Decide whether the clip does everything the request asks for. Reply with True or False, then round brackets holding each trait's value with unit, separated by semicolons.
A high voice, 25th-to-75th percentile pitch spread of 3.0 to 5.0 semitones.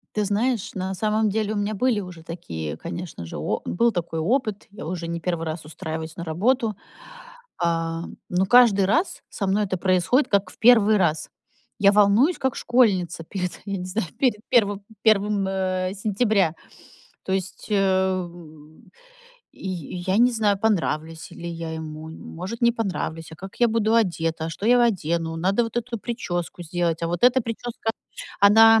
True (195 Hz; 4.6 semitones)